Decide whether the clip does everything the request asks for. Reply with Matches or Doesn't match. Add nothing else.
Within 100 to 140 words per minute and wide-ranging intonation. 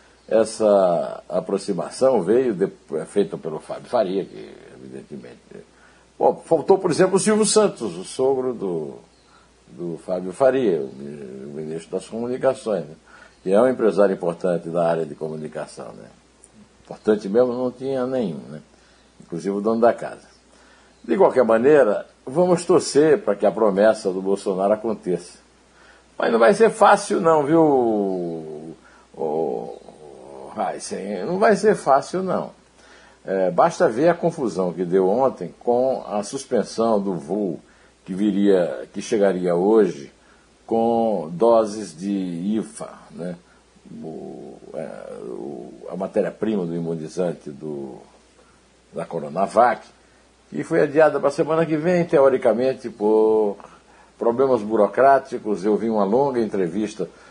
Matches